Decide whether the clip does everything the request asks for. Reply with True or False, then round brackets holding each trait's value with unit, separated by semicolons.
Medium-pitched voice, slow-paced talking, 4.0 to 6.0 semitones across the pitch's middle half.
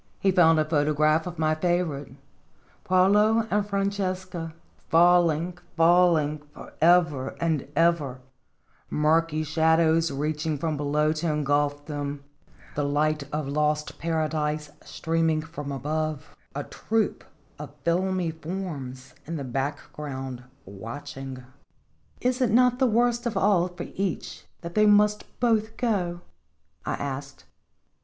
False (160 Hz; 125 wpm; 3.5 semitones)